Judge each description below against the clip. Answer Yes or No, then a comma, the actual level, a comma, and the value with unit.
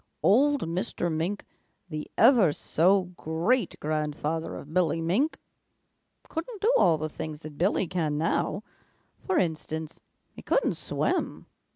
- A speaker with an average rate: No, slow, 130 wpm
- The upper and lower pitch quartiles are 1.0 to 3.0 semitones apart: No, wide, 5.4 semitones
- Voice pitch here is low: No, medium, 170 Hz